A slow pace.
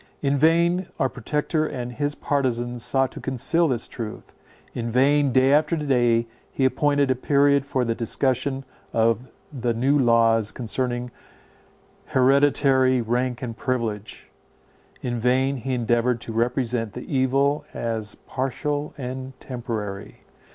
Yes: slow, 130 wpm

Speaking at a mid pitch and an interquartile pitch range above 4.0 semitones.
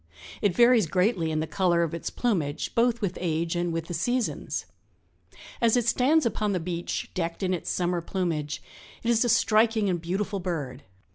Yes: medium, 180 Hz; average, 5.0 semitones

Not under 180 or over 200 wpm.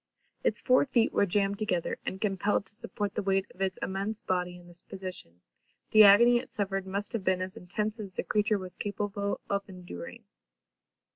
Yes: average, 190 wpm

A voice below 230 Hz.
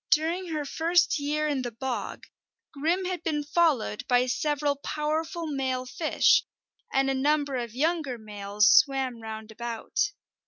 No: very high, 285 Hz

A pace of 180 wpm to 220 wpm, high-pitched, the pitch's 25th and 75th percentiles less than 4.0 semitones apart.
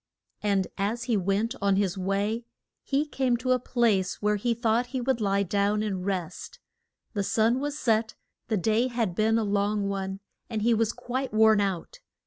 Yes: average, 185 wpm; high, 215 Hz; average, 3.1 semitones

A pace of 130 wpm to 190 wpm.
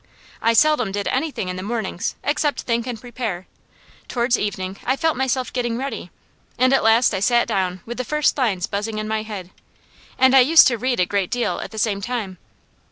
No: fast, 205 wpm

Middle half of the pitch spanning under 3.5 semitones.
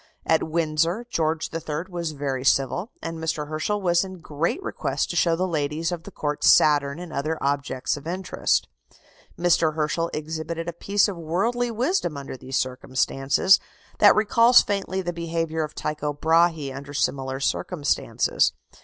Yes: average, 3.1 semitones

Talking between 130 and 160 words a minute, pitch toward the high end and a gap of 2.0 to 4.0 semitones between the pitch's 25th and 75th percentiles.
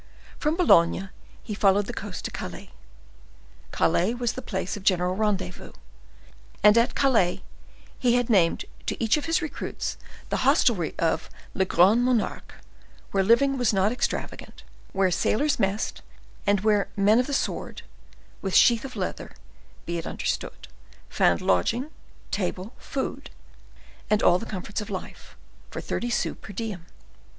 No: average, 150 wpm; high, 210 Hz; average, 4.4 semitones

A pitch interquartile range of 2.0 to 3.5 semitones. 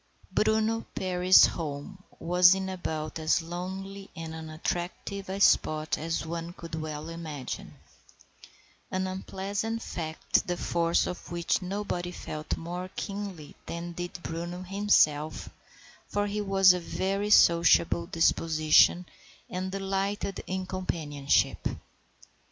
Yes: average, 2.9 semitones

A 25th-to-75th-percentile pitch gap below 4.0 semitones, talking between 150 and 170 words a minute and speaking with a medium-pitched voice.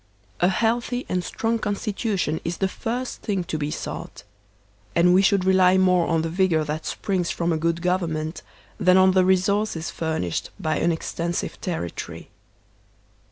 Yes: average, 2.8 semitones; average, 160 wpm; medium, 180 Hz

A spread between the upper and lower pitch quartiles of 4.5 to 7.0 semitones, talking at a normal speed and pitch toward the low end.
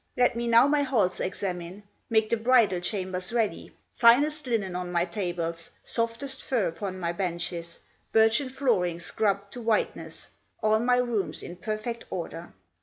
No: average, 4.8 semitones; average, 150 wpm; high, 215 Hz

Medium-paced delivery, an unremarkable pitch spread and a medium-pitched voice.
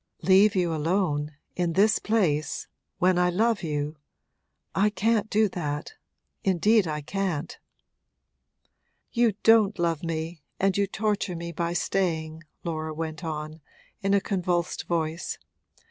No: slow, 130 wpm; average, 3.9 semitones; medium, 175 Hz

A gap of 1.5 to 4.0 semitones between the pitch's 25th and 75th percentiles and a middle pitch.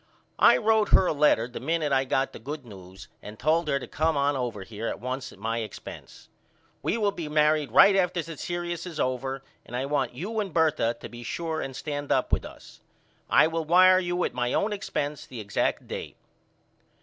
No: average, 5.2 semitones; medium, 145 Hz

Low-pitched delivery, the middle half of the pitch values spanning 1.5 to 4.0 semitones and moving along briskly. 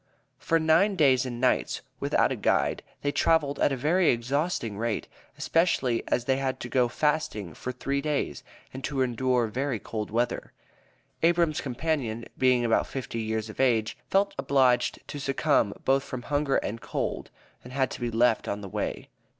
No: low, 130 Hz; average, 3.7 semitones; average, 175 wpm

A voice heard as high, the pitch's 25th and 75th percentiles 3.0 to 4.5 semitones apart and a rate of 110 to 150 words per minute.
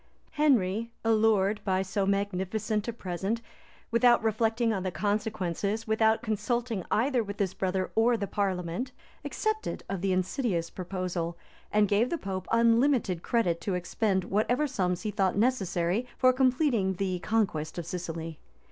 Yes: high, 205 Hz; average, 3.8 semitones; average, 145 wpm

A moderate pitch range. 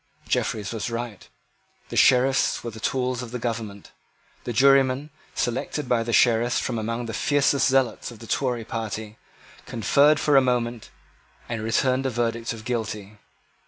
No: narrow, 2.3 semitones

